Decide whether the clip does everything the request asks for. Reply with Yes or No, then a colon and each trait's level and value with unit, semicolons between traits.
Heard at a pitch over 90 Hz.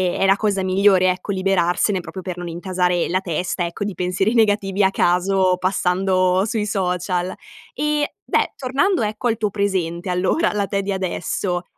Yes: high, 190 Hz